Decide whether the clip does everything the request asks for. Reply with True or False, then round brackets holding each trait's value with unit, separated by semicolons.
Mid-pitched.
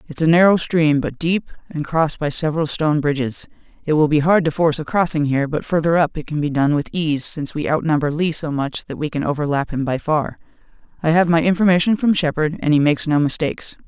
True (155 Hz)